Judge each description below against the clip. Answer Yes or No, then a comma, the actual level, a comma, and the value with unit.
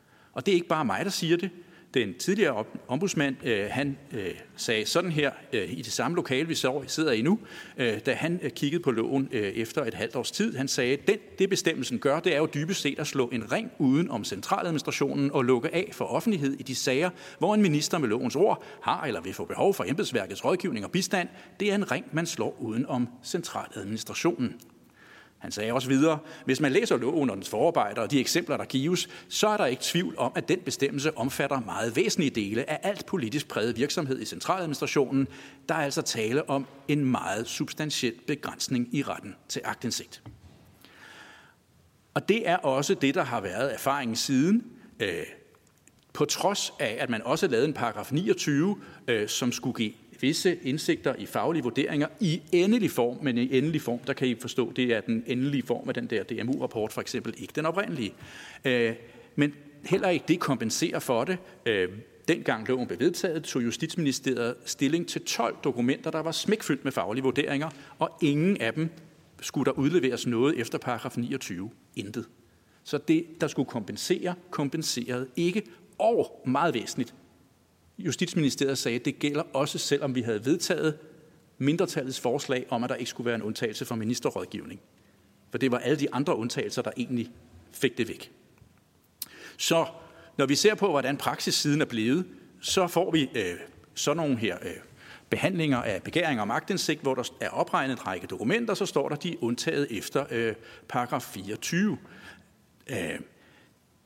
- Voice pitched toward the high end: No, medium, 140 Hz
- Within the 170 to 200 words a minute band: Yes, average, 180 wpm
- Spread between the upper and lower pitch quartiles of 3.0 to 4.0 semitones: No, average, 4.8 semitones